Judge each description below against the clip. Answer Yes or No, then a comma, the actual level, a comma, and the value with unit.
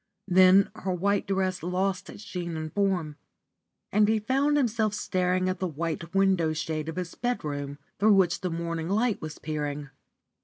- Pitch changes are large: No, average, 3.6 semitones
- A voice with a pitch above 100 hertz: Yes, medium, 185 Hz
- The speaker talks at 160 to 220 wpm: Yes, average, 165 wpm